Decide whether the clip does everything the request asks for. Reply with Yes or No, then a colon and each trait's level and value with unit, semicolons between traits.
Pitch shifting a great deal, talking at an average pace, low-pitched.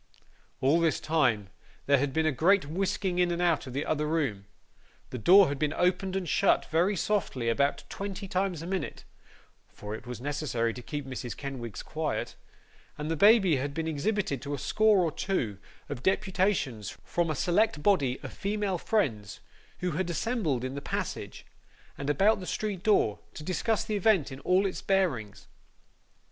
No: wide, 6.0 semitones; average, 180 wpm; medium, 160 Hz